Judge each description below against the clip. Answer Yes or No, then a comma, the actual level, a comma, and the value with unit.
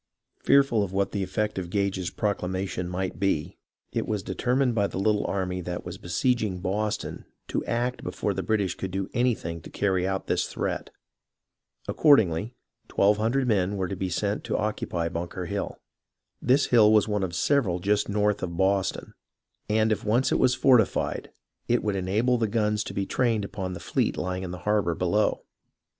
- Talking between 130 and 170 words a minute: No, average, 185 wpm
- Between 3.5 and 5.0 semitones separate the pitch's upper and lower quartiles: No, average, 2.8 semitones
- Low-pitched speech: Yes, low, 100 Hz